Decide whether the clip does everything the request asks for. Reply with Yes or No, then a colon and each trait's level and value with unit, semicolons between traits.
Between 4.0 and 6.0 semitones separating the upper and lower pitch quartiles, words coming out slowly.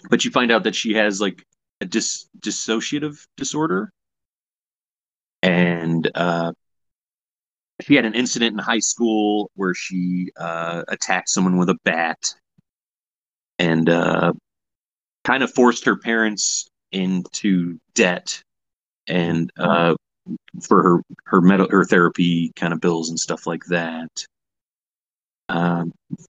Yes: average, 4.6 semitones; slow, 125 wpm